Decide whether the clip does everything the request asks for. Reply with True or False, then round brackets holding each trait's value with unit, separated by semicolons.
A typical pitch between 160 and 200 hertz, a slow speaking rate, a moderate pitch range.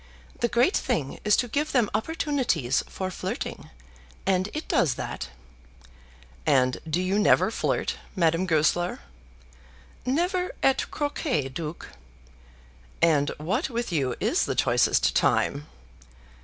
False (190 Hz; 120 wpm; 8.9 semitones)